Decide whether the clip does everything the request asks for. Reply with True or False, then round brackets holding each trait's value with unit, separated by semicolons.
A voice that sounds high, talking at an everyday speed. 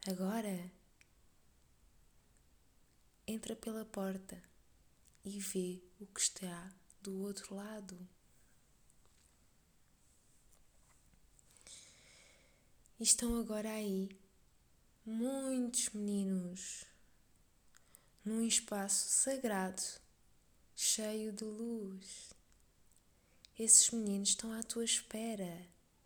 False (195 Hz; 70 wpm)